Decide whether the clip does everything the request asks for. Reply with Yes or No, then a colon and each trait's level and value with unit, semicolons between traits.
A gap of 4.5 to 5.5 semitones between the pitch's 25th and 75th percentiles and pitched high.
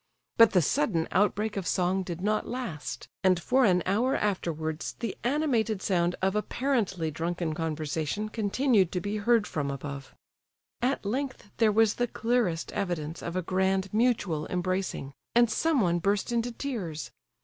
Yes: average, 5.0 semitones; high, 195 Hz